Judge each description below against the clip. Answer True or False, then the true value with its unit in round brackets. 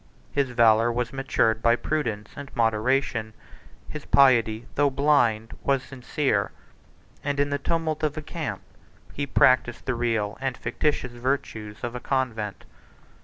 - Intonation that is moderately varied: True (3.7 semitones)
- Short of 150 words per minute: True (140 wpm)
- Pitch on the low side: True (125 Hz)